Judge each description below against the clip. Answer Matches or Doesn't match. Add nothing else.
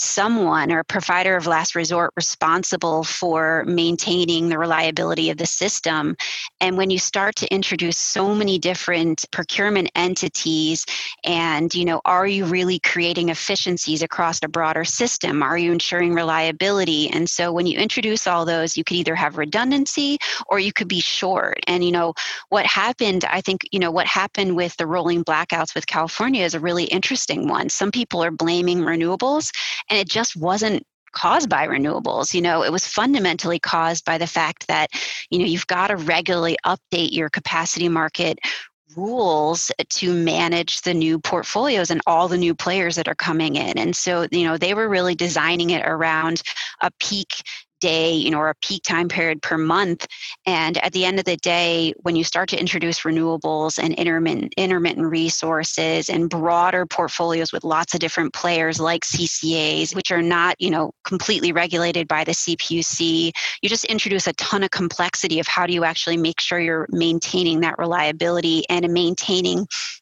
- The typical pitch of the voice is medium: Matches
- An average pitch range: Doesn't match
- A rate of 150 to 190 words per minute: Matches